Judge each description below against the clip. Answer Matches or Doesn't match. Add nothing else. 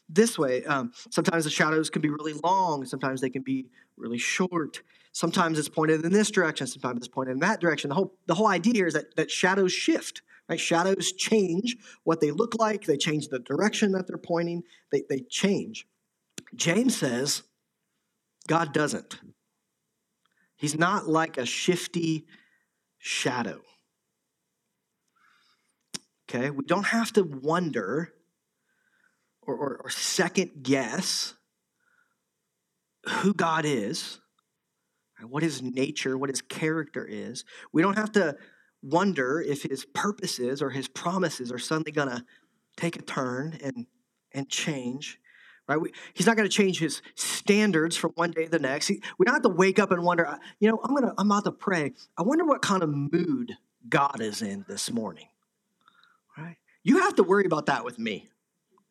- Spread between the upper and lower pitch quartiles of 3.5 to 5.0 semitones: Doesn't match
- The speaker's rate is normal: Matches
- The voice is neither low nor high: Matches